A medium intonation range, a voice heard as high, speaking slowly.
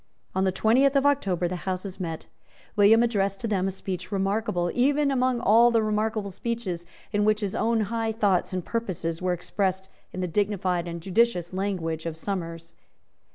No: average, 3.8 semitones; high, 195 Hz; average, 175 wpm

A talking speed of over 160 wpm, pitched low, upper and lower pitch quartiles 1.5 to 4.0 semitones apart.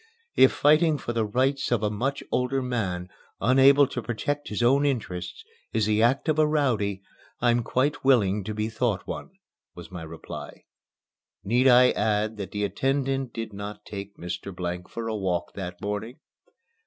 No: average, 170 wpm; low, 115 Hz; average, 4.7 semitones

